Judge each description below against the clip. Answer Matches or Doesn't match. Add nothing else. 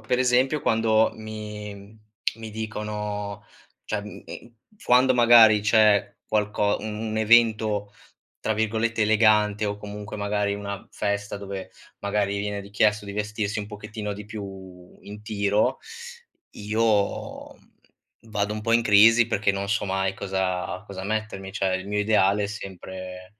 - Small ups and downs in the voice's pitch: Matches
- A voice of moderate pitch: Doesn't match